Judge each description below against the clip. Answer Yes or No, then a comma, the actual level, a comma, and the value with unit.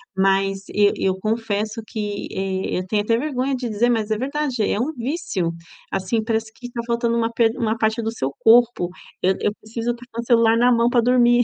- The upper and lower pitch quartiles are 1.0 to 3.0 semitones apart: Yes, narrow, 2.6 semitones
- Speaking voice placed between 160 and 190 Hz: No, high, 230 Hz